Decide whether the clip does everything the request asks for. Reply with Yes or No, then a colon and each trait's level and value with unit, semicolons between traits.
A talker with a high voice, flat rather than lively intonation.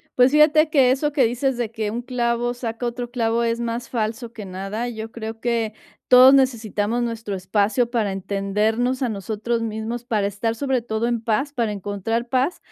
Yes: high, 230 Hz; narrow, 2.2 semitones